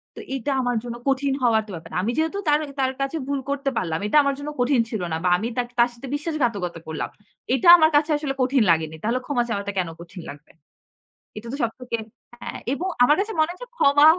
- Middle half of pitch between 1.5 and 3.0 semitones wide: No, average, 5.3 semitones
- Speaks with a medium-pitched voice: No, very high, 250 Hz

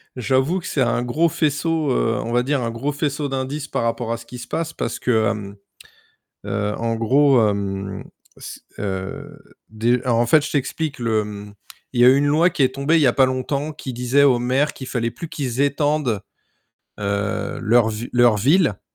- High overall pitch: No, low, 125 Hz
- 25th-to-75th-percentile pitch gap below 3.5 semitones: No, average, 4.0 semitones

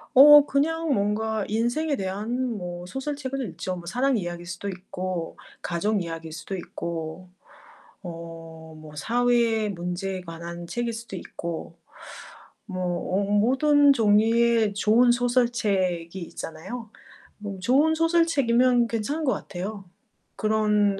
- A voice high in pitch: Yes, high, 210 Hz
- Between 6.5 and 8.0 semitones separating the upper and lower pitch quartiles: No, wide, 5.4 semitones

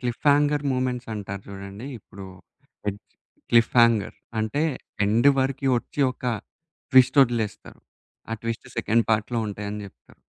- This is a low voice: Yes, low, 115 Hz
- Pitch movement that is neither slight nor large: Yes, average, 3.6 semitones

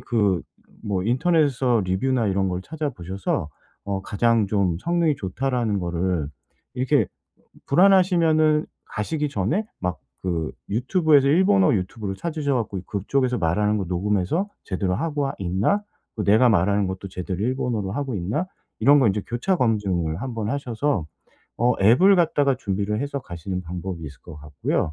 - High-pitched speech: No, low, 110 Hz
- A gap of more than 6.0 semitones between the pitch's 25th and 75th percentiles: Yes, wide, 7.0 semitones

